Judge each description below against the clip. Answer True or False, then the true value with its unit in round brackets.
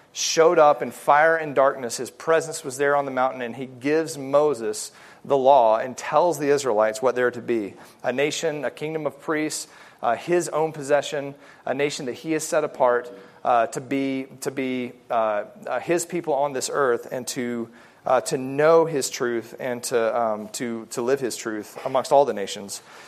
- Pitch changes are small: False (3.9 semitones)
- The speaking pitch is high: False (135 Hz)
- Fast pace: False (190 wpm)